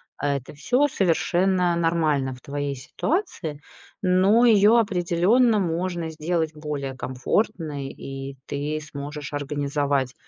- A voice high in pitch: No, medium, 155 Hz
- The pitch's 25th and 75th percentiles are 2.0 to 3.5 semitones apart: No, average, 4.6 semitones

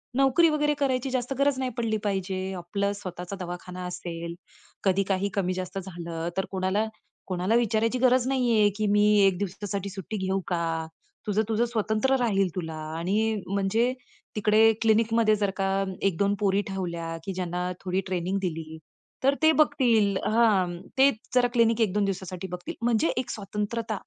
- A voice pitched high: Yes, high, 200 Hz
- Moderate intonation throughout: Yes, average, 3.8 semitones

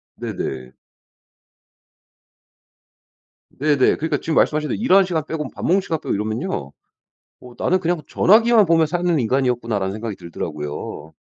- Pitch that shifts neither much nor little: No, wide, 8.3 semitones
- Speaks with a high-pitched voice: No, medium, 150 Hz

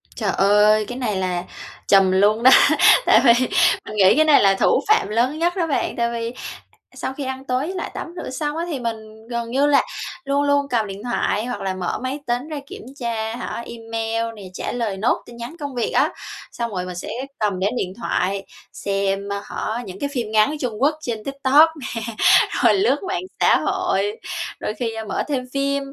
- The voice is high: Yes, high, 235 Hz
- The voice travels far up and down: No, average, 4.9 semitones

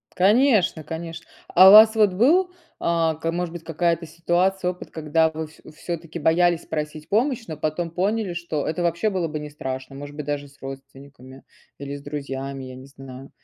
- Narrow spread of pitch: No, average, 3.6 semitones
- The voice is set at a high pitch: No, medium, 160 Hz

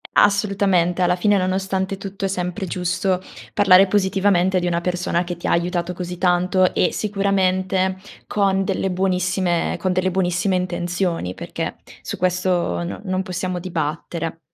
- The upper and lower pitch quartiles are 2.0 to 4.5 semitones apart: No, narrow, 1.4 semitones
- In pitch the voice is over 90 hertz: Yes, medium, 185 Hz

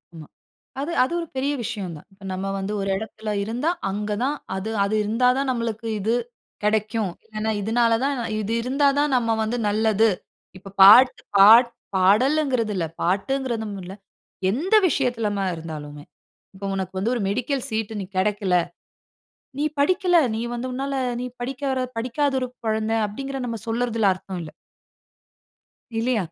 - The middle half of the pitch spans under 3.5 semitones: No, average, 4.2 semitones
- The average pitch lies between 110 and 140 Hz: No, high, 225 Hz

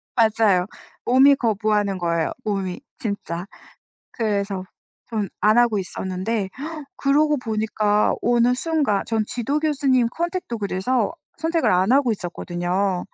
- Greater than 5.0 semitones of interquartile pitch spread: No, average, 4.5 semitones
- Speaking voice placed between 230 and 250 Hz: No, high, 215 Hz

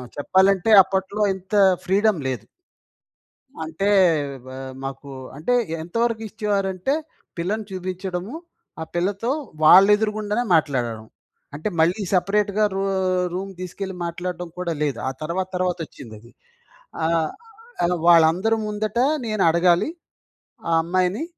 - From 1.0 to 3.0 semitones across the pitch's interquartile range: No, average, 3.7 semitones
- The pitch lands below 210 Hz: Yes, medium, 185 Hz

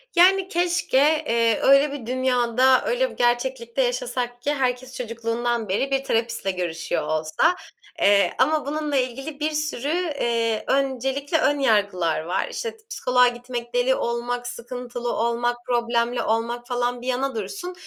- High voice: Yes, high, 245 Hz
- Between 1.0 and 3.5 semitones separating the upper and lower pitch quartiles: Yes, narrow, 2.6 semitones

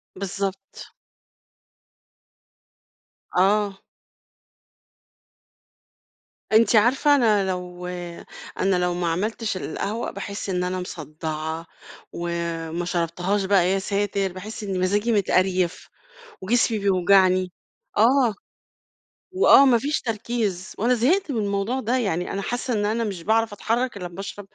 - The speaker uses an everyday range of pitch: Yes, average, 3.7 semitones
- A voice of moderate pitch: No, high, 200 Hz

